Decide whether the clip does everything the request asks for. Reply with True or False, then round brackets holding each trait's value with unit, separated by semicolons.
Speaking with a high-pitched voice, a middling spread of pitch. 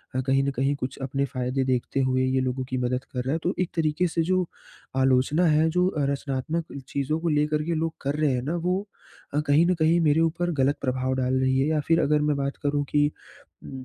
False (145 Hz; 3.4 semitones)